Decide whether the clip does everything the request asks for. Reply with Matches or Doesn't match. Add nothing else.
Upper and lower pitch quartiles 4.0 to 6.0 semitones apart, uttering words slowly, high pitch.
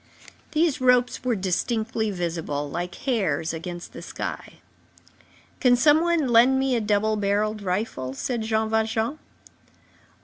Matches